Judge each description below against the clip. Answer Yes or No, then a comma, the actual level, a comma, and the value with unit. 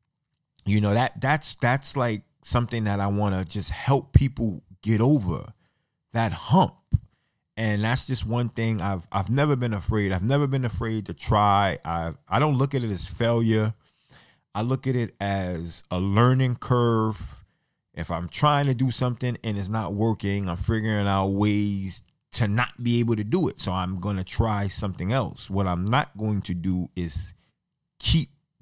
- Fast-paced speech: No, average, 180 wpm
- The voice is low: Yes, low, 110 Hz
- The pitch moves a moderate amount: Yes, average, 3.9 semitones